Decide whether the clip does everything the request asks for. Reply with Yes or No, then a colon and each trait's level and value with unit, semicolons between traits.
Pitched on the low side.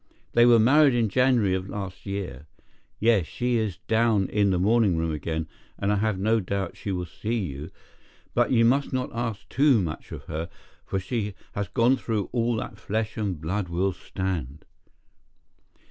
Yes: low, 105 Hz